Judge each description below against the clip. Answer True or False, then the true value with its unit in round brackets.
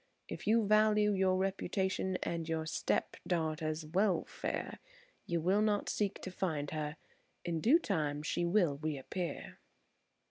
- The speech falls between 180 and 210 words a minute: False (135 wpm)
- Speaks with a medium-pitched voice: True (175 Hz)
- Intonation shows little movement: False (4.1 semitones)